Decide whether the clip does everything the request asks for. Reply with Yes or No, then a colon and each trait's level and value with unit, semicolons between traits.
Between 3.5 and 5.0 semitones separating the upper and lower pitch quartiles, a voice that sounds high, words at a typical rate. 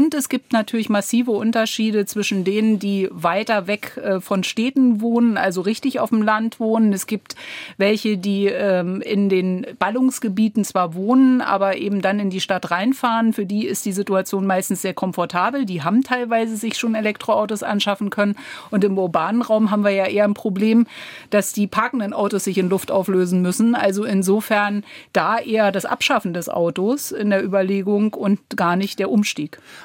No: narrow, 2.5 semitones; high, 205 Hz; average, 175 wpm